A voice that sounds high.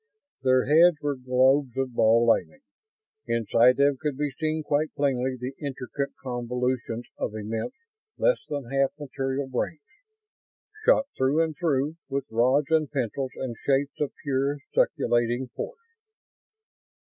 No: low, 135 Hz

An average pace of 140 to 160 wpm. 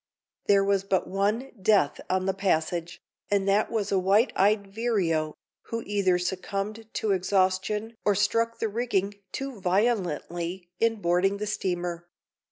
Yes: average, 145 wpm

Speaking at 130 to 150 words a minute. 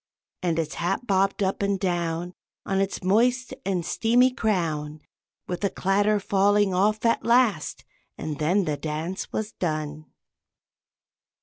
Yes: slow, 135 wpm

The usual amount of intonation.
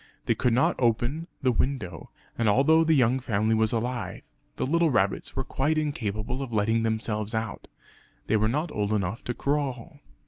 Yes: average, 4.1 semitones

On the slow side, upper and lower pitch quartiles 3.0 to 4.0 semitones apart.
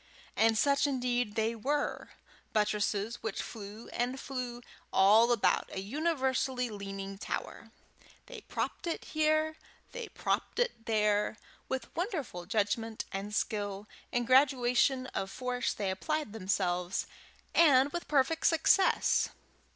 No: slow, 120 wpm; average, 5.2 semitones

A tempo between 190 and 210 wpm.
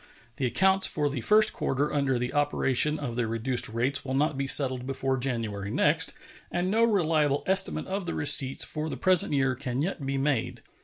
Yes: average, 195 wpm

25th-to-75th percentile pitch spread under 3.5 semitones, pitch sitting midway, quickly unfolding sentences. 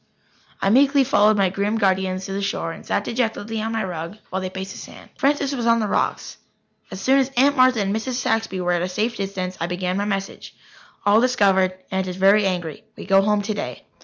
No: average, 3.1 semitones; high, 200 Hz; fast, 220 wpm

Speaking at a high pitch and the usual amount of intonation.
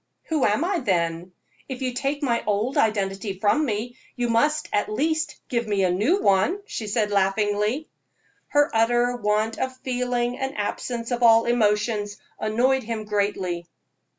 Yes: high, 230 Hz; average, 3.8 semitones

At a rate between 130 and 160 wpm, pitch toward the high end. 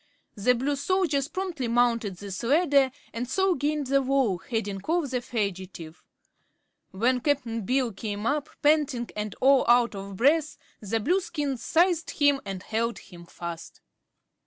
Yes: average, 145 wpm; very high, 250 Hz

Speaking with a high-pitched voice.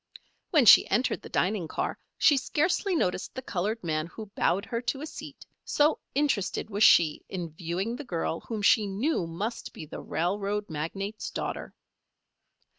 Yes: high, 205 Hz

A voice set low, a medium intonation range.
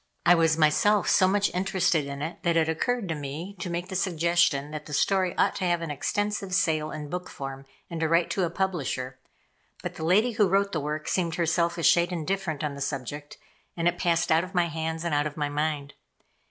No: medium, 165 Hz; average, 3.2 semitones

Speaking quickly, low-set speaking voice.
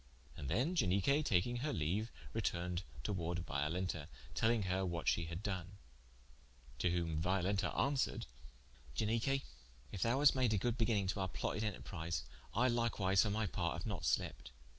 No: average, 160 wpm; very low, 95 Hz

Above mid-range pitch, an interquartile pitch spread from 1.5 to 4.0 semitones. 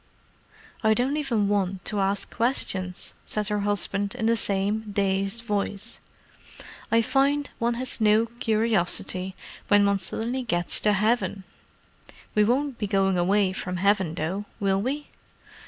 Yes: high, 205 Hz; average, 3.0 semitones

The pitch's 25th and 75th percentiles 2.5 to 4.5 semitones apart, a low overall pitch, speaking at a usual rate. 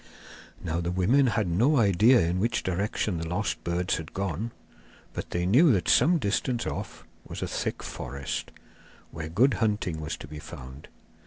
No: wide, 5.4 semitones; very low, 95 Hz; average, 170 wpm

